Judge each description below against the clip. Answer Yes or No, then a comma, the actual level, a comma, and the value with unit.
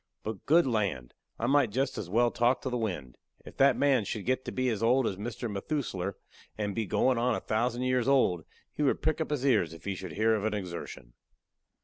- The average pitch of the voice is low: Yes, low, 115 Hz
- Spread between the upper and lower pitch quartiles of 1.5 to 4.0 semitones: No, average, 4.5 semitones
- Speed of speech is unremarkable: No, fast, 230 wpm